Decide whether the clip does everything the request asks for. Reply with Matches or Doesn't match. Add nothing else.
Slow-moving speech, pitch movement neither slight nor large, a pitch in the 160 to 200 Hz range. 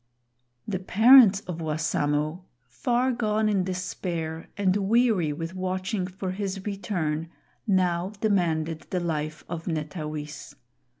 Matches